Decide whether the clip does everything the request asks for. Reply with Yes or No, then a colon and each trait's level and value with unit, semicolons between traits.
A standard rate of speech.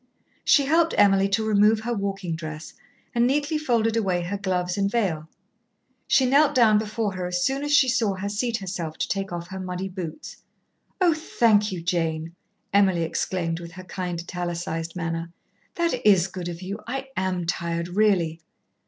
Yes: average, 175 wpm